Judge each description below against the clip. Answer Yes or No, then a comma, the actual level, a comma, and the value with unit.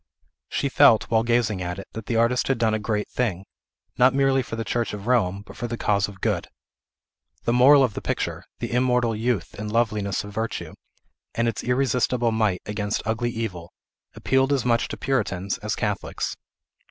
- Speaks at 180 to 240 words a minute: Yes, average, 190 wpm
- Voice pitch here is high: No, low, 115 Hz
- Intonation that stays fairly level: No, average, 3.0 semitones